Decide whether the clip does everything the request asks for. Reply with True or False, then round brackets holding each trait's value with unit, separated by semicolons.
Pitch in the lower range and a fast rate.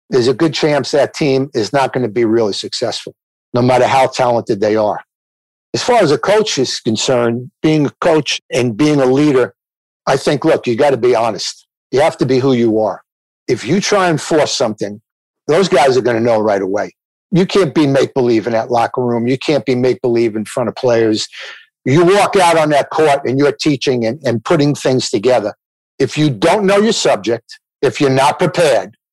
True (130 Hz; 215 wpm)